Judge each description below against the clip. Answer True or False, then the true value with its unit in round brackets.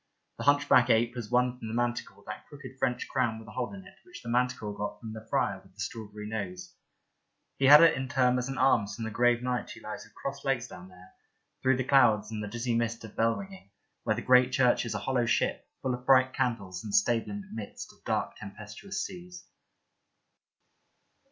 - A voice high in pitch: False (120 Hz)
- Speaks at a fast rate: True (220 wpm)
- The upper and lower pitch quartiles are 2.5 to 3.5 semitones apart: True (3.2 semitones)